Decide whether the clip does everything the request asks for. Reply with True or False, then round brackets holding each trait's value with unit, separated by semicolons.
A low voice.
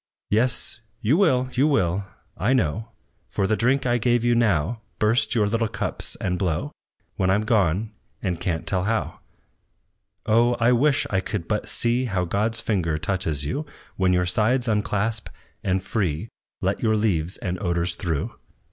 True (105 Hz)